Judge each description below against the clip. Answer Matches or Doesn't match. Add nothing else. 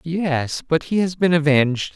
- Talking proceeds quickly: Doesn't match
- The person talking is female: Doesn't match